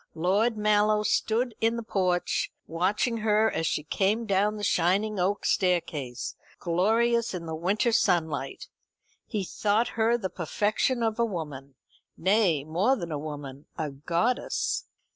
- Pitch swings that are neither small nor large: Yes, average, 4.9 semitones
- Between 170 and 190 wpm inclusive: No, average, 140 wpm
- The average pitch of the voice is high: Yes, high, 195 Hz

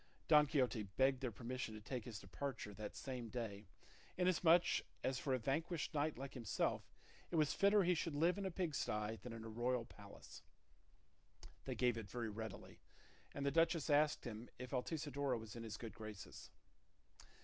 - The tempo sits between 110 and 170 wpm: No, average, 180 wpm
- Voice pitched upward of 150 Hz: No, low, 125 Hz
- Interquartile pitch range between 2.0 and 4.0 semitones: No, average, 5.1 semitones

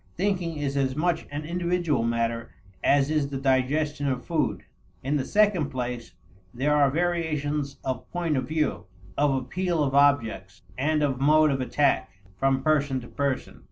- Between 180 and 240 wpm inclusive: No, average, 160 wpm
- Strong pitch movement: No, average, 2.9 semitones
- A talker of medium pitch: Yes, medium, 145 Hz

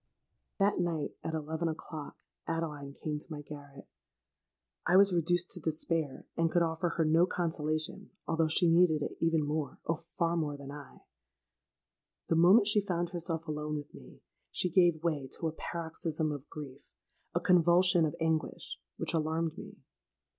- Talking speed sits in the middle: Yes, average, 155 wpm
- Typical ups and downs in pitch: No, narrow, 2.1 semitones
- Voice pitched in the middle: Yes, medium, 160 Hz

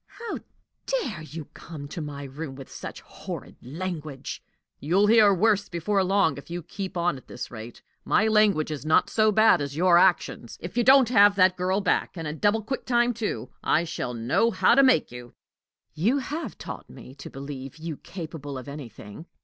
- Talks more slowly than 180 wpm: No, average, 190 wpm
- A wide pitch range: Yes, wide, 6.4 semitones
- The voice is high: No, medium, 175 Hz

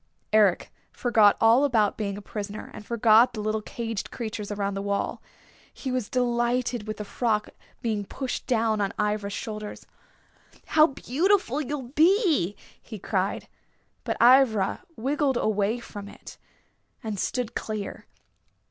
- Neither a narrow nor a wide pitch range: Yes, average, 3.2 semitones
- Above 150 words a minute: No, average, 140 wpm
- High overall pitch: Yes, high, 220 Hz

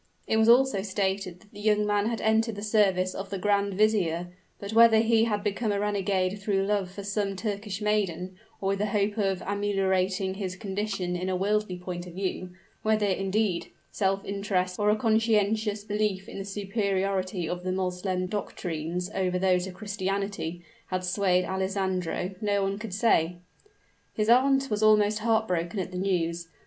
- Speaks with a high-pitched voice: Yes, high, 195 Hz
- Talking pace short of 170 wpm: No, average, 175 wpm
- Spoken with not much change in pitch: Yes, narrow, 2.2 semitones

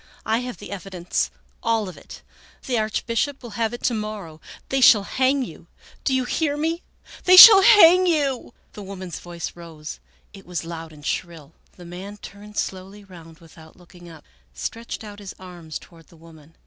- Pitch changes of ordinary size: No, wide, 6.1 semitones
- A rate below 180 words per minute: No, average, 185 wpm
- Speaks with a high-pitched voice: Yes, high, 200 Hz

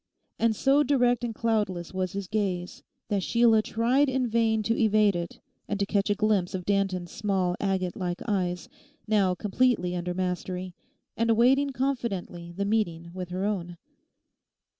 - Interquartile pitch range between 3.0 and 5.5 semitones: Yes, average, 4.0 semitones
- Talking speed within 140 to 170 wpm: Yes, average, 160 wpm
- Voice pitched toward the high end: Yes, high, 200 Hz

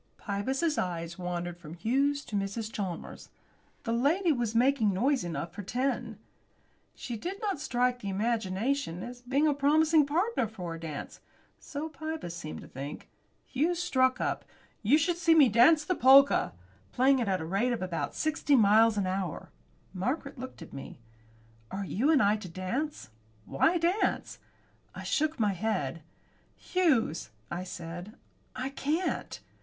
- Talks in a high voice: Yes, high, 240 Hz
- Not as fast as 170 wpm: Yes, average, 155 wpm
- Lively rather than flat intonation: Yes, wide, 7.5 semitones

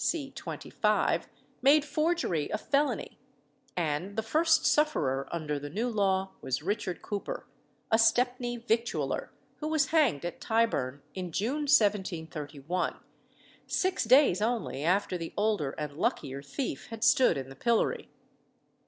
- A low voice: No, high, 210 Hz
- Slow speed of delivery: Yes, slow, 130 wpm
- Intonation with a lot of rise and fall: Yes, wide, 7.9 semitones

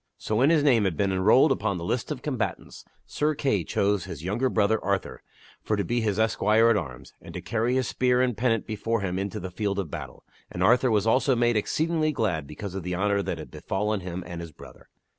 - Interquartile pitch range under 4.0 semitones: No, average, 4.4 semitones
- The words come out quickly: Yes, fast, 230 wpm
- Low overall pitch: Yes, low, 105 Hz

